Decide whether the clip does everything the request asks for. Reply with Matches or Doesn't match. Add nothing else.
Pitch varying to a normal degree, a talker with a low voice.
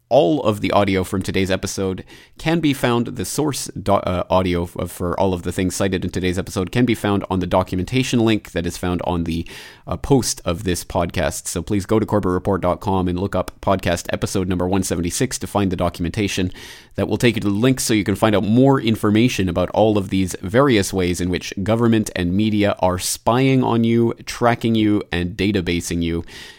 Matches